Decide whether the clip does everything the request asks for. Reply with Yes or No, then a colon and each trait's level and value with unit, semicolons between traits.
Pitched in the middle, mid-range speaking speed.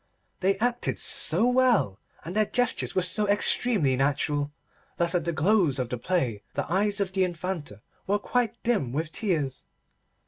Yes: medium, 180 Hz; average, 165 wpm